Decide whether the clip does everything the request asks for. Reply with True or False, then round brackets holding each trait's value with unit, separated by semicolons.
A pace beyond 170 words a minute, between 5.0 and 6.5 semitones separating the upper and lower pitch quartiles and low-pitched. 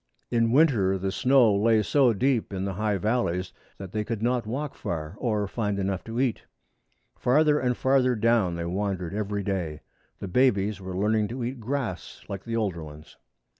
False (180 wpm; 4.2 semitones; 105 Hz)